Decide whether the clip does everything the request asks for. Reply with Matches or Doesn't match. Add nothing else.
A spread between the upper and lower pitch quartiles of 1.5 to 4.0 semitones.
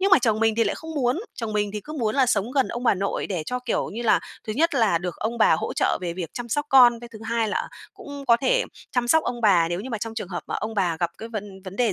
Matches